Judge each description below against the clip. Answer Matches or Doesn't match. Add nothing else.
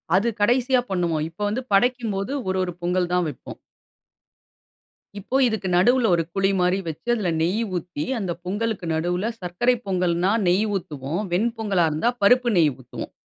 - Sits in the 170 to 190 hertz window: Matches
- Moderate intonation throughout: Matches